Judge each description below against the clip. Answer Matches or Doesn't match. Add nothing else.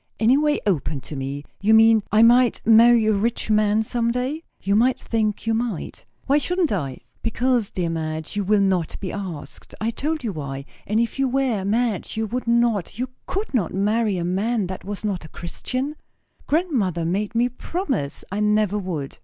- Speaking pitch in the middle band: Doesn't match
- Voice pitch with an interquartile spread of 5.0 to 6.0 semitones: Doesn't match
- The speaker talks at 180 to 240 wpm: Matches